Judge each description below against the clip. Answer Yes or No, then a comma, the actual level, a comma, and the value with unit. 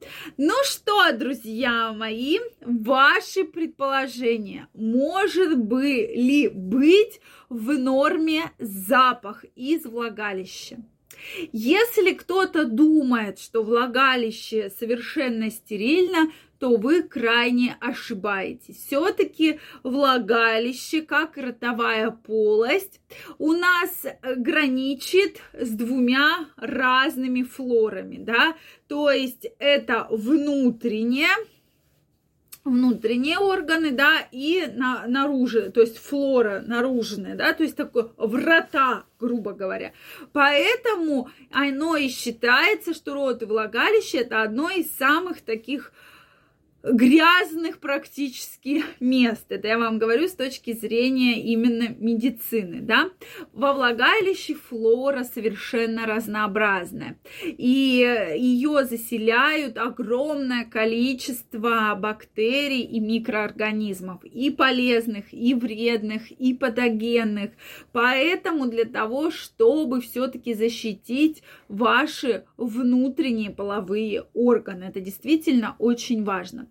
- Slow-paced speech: Yes, slow, 95 wpm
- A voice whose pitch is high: Yes, very high, 255 Hz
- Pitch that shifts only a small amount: No, average, 4.6 semitones